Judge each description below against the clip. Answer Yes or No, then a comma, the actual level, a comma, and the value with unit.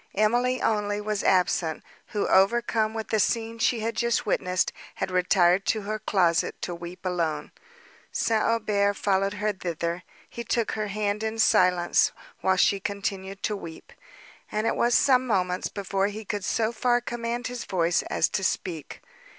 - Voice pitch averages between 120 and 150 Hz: No, high, 205 Hz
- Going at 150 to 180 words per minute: Yes, average, 165 wpm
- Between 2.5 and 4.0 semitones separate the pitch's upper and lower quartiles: Yes, average, 3.4 semitones